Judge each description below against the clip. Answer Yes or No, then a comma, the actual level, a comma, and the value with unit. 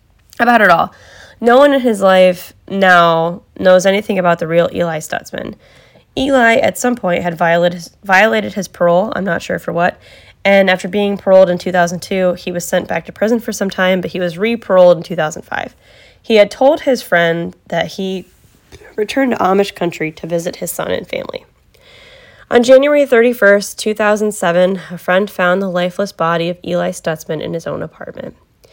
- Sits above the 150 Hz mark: Yes, high, 190 Hz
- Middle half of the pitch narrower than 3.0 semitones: No, average, 3.9 semitones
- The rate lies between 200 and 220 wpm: No, average, 175 wpm